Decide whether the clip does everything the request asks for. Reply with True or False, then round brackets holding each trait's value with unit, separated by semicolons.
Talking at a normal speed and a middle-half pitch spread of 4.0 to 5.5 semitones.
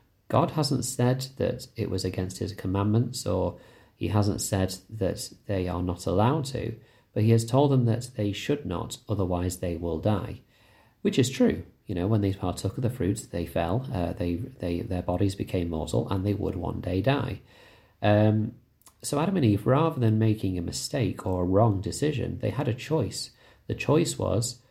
True (190 wpm; 4.6 semitones)